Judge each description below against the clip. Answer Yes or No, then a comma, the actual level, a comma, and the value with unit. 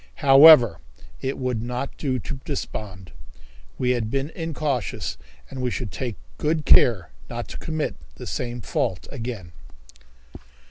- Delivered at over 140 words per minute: No, slow, 135 wpm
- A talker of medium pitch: No, low, 125 Hz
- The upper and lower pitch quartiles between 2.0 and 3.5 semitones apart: No, average, 3.9 semitones